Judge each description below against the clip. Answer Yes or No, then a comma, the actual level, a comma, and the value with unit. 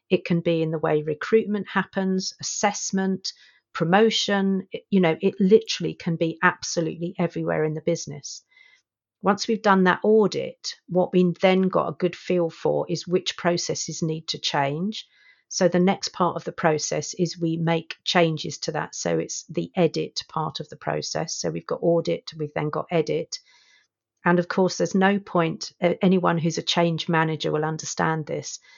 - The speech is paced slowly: No, average, 175 wpm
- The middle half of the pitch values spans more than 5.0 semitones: No, average, 3.0 semitones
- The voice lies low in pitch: No, medium, 175 Hz